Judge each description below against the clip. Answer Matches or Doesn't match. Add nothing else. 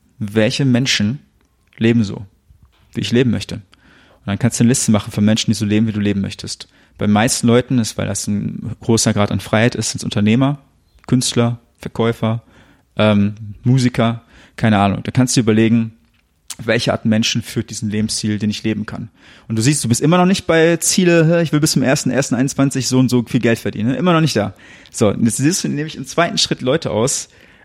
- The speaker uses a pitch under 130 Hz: Matches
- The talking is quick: Matches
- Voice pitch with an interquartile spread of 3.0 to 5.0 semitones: Matches